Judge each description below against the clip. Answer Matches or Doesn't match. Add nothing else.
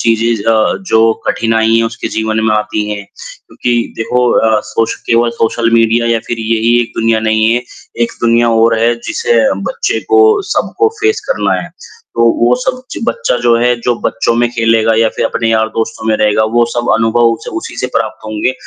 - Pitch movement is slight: Matches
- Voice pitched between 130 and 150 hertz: Doesn't match